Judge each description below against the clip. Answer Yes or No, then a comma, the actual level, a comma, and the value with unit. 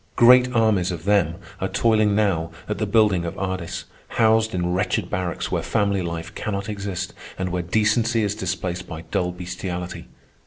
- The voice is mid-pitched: No, very low, 95 Hz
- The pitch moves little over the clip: No, average, 3.3 semitones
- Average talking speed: Yes, average, 165 wpm